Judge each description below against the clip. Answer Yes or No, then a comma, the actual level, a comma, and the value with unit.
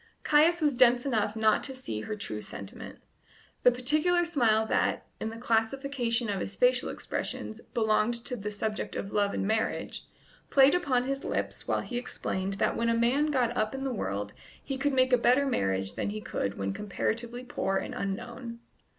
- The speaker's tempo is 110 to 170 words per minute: No, average, 185 wpm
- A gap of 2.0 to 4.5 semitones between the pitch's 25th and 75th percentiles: Yes, average, 4.1 semitones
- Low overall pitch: No, high, 235 Hz